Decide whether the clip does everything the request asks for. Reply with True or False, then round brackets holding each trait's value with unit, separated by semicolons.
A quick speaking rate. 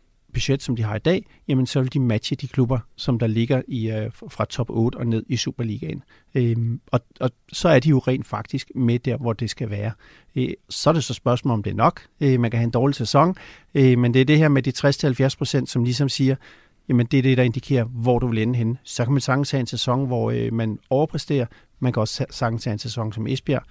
True (255 wpm)